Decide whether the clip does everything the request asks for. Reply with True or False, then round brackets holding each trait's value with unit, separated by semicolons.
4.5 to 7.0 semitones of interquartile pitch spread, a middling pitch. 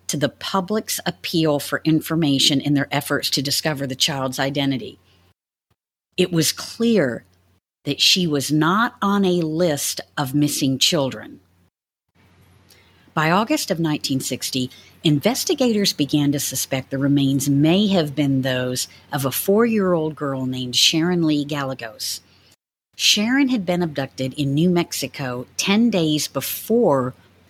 True (4.8 semitones; 145 Hz)